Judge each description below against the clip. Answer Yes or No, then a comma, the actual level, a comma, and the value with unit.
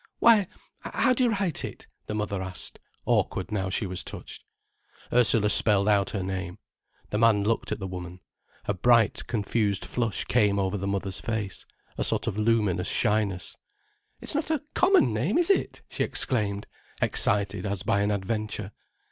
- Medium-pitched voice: No, low, 105 Hz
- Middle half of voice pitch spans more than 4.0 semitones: No, average, 2.9 semitones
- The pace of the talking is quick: No, average, 165 wpm